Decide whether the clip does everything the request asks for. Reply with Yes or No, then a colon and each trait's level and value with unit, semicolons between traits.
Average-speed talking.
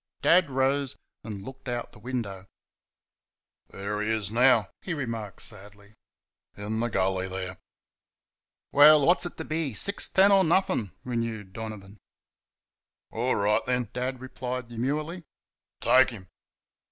No: slow, 130 wpm